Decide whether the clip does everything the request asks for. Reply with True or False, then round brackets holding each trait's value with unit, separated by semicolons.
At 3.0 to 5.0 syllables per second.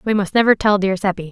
False (6.6 syllables/s)